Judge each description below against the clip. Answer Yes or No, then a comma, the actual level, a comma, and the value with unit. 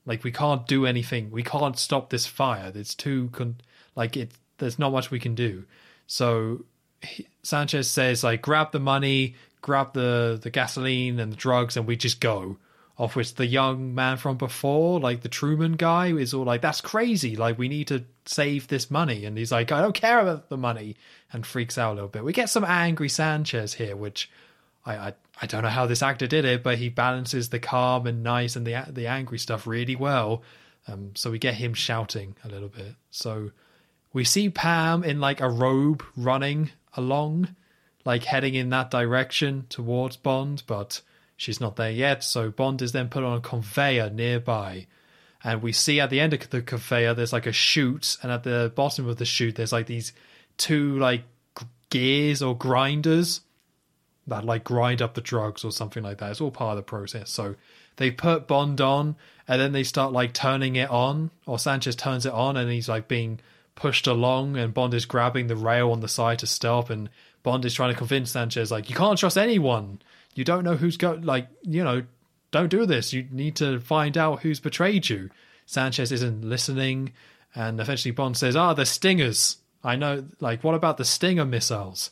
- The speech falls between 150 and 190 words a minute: No, average, 200 wpm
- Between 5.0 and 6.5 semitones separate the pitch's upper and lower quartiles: No, average, 3.2 semitones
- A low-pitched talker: Yes, low, 125 Hz